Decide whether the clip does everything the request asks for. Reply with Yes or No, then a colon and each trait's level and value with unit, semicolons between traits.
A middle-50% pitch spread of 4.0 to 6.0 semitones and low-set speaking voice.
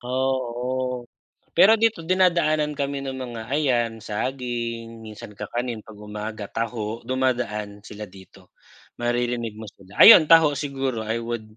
No: average, 3.4 semitones; low, 120 Hz